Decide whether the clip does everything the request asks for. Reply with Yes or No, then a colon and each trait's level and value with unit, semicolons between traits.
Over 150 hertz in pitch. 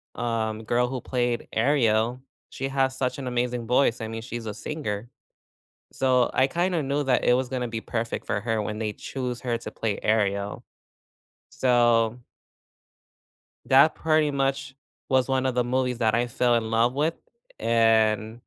No: low, 120 Hz